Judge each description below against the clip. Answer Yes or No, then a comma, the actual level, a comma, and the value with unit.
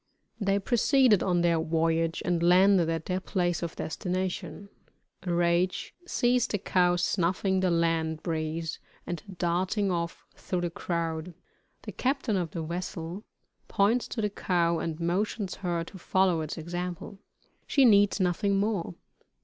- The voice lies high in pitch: No, medium, 175 Hz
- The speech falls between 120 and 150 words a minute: Yes, average, 140 wpm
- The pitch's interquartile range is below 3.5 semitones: Yes, average, 2.8 semitones